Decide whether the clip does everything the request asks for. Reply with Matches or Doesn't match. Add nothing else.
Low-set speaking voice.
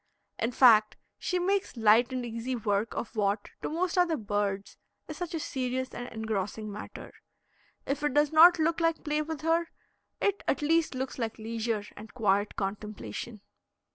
Doesn't match